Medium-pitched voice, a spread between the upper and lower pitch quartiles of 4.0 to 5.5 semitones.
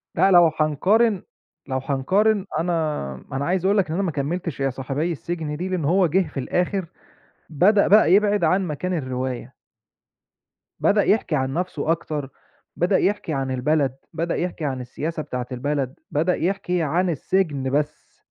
Yes: medium, 165 Hz; average, 4.7 semitones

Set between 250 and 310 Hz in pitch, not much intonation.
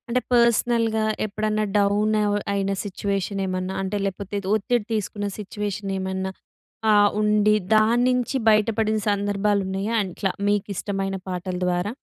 No: high, 205 Hz; narrow, 1.7 semitones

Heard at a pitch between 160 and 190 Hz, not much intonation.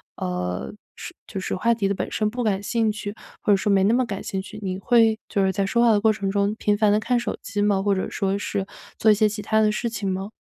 No: high, 205 Hz; narrow, 1.9 semitones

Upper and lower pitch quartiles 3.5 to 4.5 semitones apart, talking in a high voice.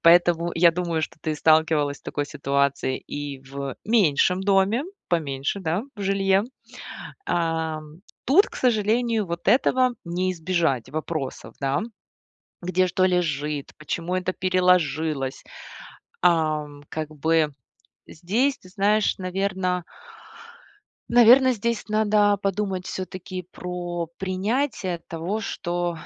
No: average, 3.9 semitones; medium, 180 Hz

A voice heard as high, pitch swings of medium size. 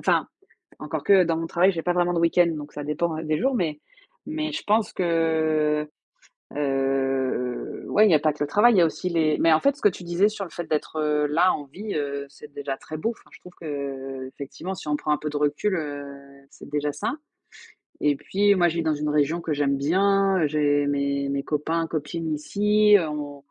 No: medium, 155 Hz; average, 3.6 semitones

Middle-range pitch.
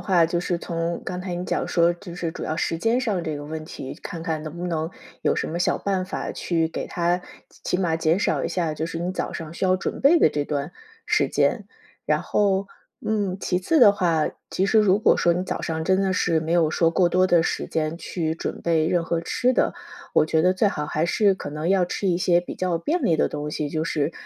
Yes: medium, 170 Hz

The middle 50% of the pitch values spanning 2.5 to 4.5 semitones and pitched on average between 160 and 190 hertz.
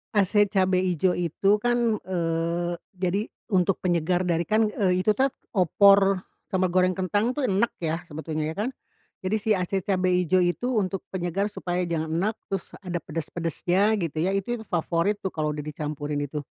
Yes: average, 2.9 semitones; medium, 185 Hz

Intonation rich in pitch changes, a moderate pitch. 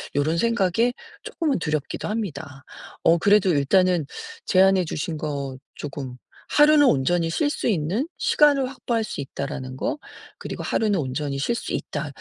Yes: wide, 8.2 semitones; medium, 175 Hz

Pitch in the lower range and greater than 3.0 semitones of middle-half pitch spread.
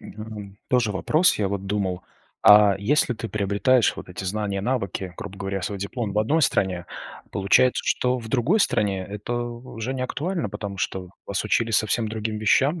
Yes: low, 105 Hz; average, 3.7 semitones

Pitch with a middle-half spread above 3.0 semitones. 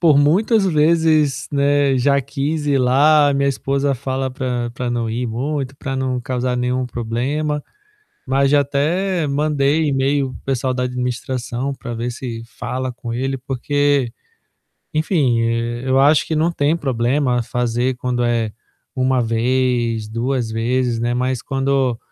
No: average, 2.7 semitones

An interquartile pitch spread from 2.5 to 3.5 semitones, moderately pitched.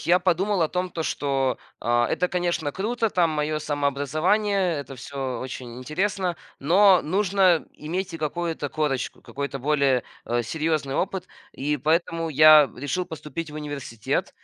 No: average, 4.2 semitones; medium, 155 Hz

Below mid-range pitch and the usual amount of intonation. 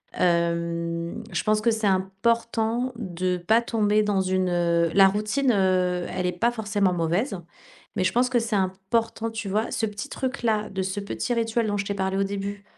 No: high, 200 Hz; average, 3.4 semitones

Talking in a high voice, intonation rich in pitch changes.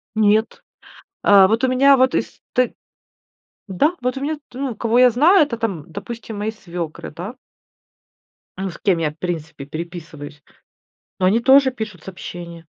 Yes: high, 210 Hz; wide, 6.5 semitones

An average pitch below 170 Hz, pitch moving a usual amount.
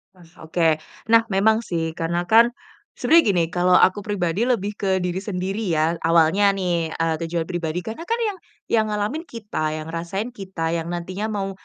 No: medium, 185 Hz; average, 4.1 semitones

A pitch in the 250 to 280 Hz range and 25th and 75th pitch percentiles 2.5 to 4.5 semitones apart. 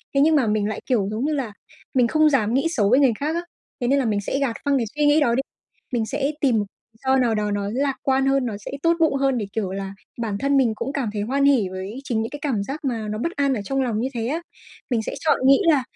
Yes: very high, 255 Hz; average, 4.2 semitones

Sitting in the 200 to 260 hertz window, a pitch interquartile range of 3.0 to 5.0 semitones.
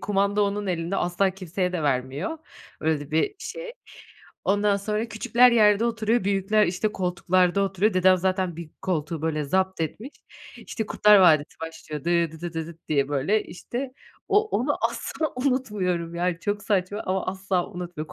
No: medium, 185 Hz; average, 3.8 semitones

